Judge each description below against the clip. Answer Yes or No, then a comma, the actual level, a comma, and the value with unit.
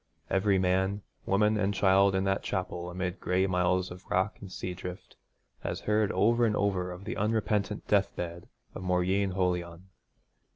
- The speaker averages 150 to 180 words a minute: Yes, average, 160 wpm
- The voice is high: No, very low, 95 Hz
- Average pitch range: No, narrow, 1.8 semitones